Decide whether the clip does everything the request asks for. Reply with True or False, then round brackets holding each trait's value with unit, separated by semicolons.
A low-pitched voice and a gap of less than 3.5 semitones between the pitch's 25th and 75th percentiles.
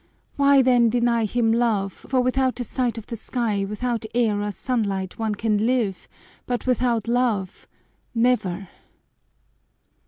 False (230 Hz; 3.1 semitones)